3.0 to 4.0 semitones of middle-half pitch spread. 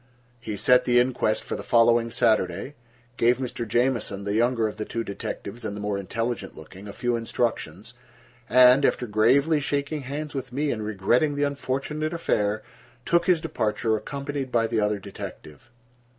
No: average, 4.4 semitones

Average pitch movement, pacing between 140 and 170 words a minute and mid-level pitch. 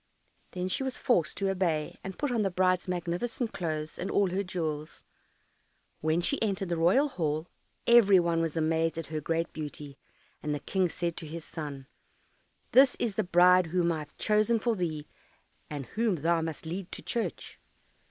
No: average, 3.5 semitones; average, 180 wpm; medium, 175 Hz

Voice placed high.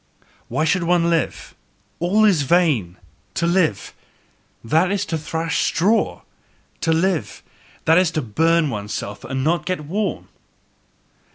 No: medium, 165 Hz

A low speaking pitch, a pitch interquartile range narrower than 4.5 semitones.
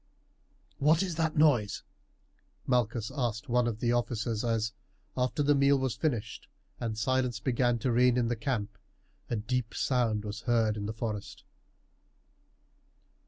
Yes: low, 120 Hz; average, 2.8 semitones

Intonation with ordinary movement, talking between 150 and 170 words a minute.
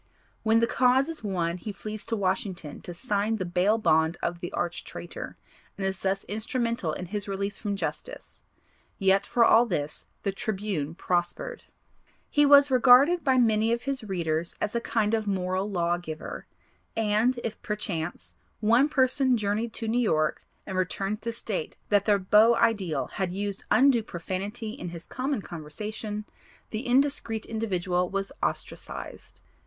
Yes: average, 4.2 semitones; average, 160 wpm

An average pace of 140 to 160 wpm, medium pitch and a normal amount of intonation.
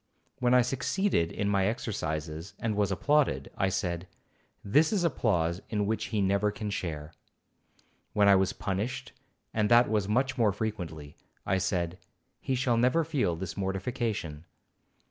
No: average, 150 wpm; low, 100 Hz; average, 4.9 semitones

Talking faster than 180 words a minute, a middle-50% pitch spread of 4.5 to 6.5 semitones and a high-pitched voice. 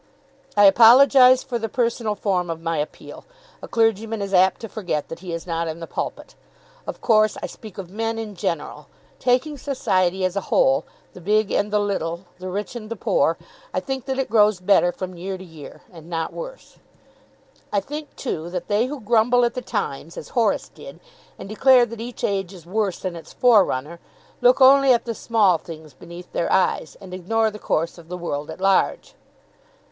Yes: average, 200 wpm; average, 4.9 semitones; high, 200 Hz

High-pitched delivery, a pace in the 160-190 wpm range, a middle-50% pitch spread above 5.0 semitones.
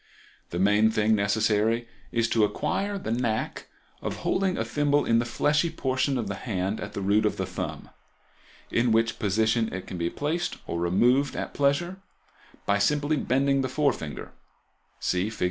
No: low, 115 Hz; average, 170 wpm; wide, 5.4 semitones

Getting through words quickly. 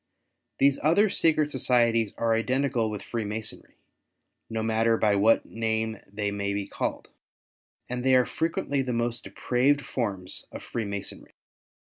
No: slow, 135 wpm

